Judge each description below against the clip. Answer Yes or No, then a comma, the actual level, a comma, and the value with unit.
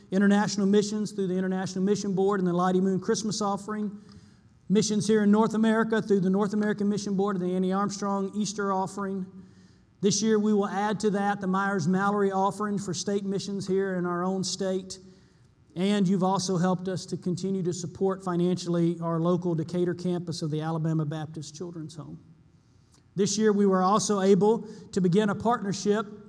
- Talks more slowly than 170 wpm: No, average, 180 wpm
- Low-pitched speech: No, high, 195 Hz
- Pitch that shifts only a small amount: Yes, narrow, 2.3 semitones